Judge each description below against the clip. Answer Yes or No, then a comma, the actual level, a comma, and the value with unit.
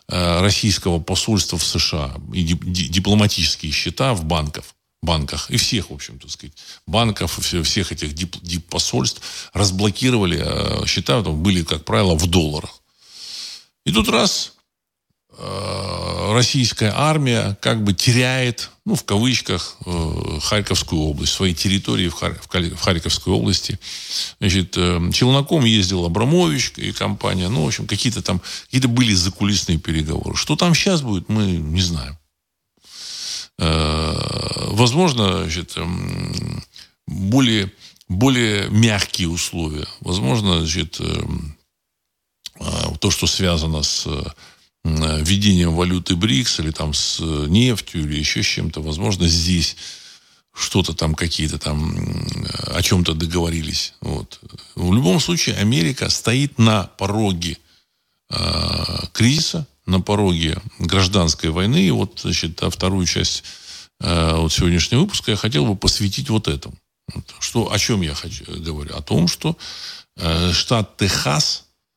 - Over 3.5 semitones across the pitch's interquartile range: Yes, average, 4.4 semitones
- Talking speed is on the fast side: No, average, 115 wpm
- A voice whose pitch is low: Yes, very low, 90 Hz